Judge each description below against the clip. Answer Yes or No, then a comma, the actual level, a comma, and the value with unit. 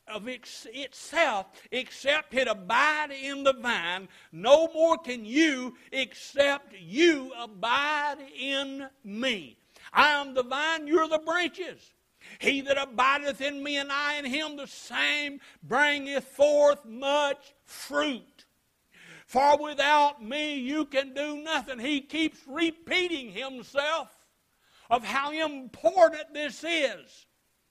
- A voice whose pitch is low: No, very high, 280 Hz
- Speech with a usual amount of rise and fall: No, narrow, 2.2 semitones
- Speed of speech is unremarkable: No, slow, 120 wpm